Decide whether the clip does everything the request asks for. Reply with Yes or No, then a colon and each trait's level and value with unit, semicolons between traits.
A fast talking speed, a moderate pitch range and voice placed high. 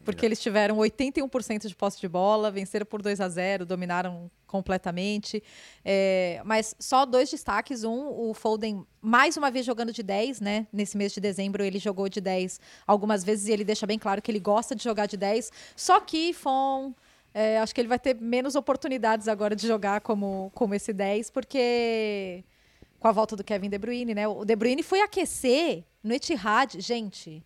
Yes: fast, 190 wpm; average, 3.2 semitones; high, 215 Hz